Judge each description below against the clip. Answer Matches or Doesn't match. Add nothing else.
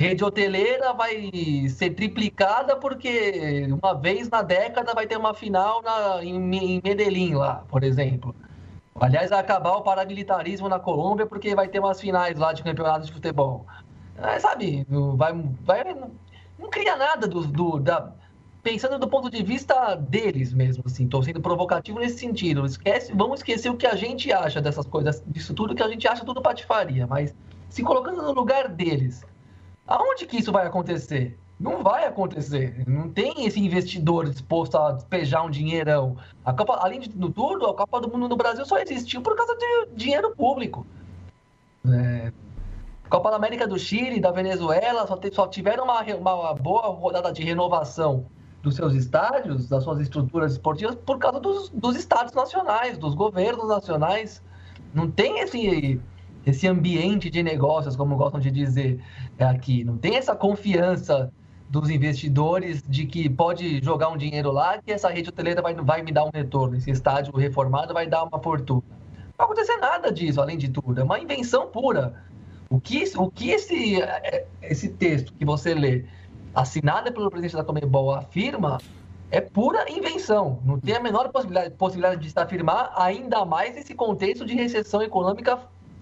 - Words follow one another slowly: Doesn't match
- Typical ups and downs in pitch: Doesn't match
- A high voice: Doesn't match